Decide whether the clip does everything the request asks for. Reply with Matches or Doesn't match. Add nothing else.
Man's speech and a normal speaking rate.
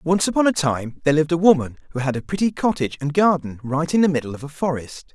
Doesn't match